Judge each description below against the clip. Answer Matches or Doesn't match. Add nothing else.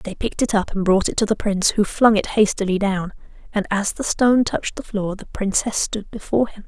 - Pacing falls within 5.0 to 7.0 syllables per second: Matches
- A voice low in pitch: Doesn't match